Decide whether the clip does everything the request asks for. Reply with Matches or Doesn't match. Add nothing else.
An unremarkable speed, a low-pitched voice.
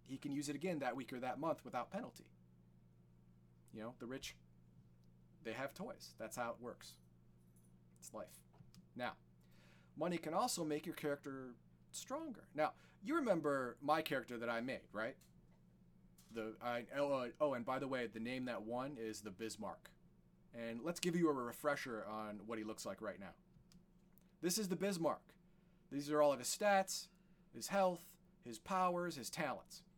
Matches